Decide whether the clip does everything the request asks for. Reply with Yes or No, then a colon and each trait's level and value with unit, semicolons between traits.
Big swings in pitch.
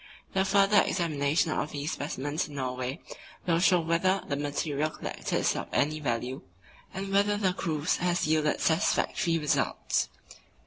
No: average, 4.2 semitones